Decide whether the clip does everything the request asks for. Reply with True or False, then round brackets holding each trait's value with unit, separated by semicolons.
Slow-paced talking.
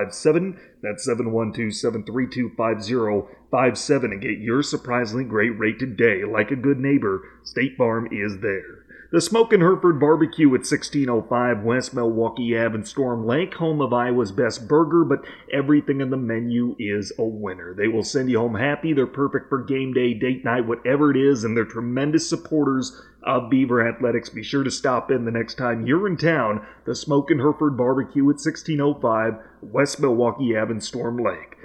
False (190 wpm)